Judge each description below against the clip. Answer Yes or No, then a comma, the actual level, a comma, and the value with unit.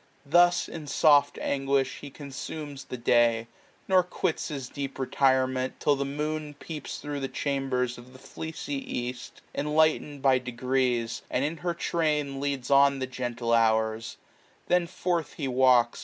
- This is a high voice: No, low, 135 Hz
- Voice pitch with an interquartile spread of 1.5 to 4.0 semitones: Yes, average, 2.8 semitones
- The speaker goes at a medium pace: Yes, average, 155 wpm